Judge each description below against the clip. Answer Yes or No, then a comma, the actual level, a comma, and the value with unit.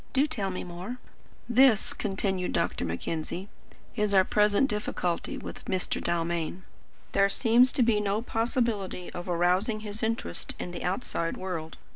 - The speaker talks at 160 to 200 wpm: No, average, 145 wpm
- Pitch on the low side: No, high, 195 Hz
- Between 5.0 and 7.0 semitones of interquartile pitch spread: No, average, 4.0 semitones